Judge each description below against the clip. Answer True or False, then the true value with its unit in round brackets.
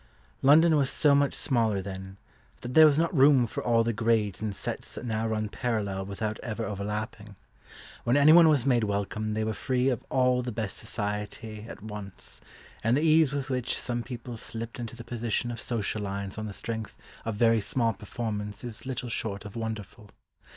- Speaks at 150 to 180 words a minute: False (190 wpm)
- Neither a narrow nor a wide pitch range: True (3.1 semitones)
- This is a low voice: True (115 Hz)